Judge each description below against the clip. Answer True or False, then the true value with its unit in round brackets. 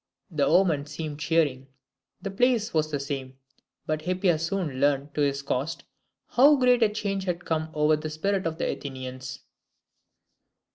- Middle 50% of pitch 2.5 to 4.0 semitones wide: False (5.1 semitones)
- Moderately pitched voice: True (155 Hz)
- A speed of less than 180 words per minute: True (155 wpm)